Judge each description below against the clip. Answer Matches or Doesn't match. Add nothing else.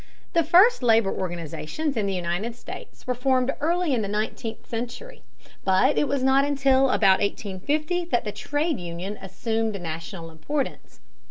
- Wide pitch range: Matches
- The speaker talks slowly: Doesn't match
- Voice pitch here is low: Doesn't match